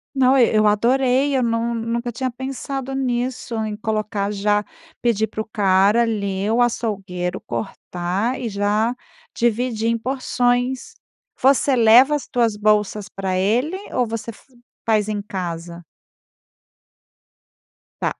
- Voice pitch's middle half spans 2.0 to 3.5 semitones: Yes, average, 3.1 semitones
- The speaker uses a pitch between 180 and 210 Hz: No, high, 225 Hz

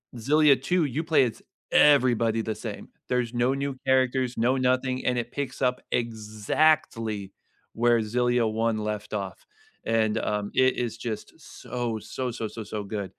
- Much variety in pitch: No, average, 2.8 semitones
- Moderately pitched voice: No, low, 120 Hz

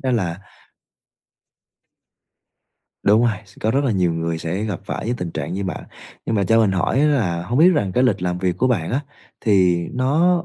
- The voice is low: Yes, low, 100 Hz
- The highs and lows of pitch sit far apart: Yes, wide, 5.9 semitones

